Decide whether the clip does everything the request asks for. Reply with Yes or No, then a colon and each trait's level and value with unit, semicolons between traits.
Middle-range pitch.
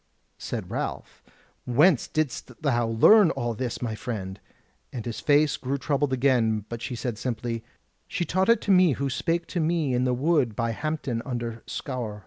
No: low, 125 Hz